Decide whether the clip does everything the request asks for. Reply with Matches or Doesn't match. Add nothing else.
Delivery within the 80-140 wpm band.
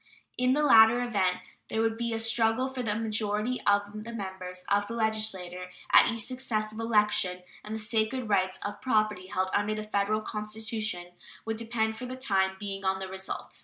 Doesn't match